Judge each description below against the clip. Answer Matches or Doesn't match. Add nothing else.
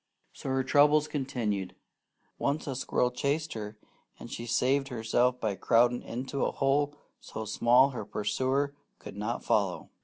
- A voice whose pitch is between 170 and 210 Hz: Doesn't match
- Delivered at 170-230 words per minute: Doesn't match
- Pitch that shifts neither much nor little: Matches